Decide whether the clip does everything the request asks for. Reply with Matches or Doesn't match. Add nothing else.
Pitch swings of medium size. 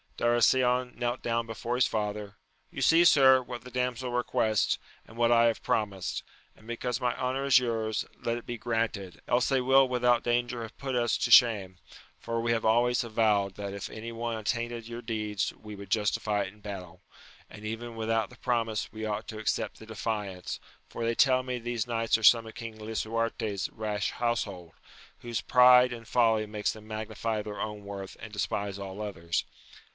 Doesn't match